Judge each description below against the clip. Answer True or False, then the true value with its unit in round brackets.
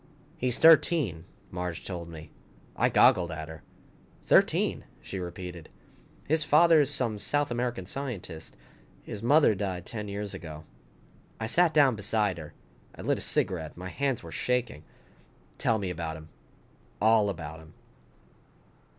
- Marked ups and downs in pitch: True (6.8 semitones)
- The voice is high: False (100 Hz)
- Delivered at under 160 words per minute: True (140 wpm)